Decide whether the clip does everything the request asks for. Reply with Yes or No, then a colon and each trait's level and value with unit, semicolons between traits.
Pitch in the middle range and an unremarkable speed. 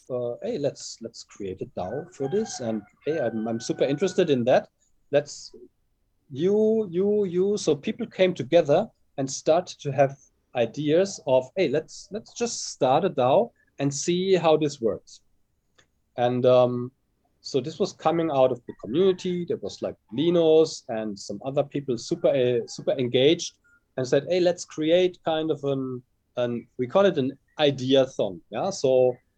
Yes: medium, 145 Hz; average, 170 wpm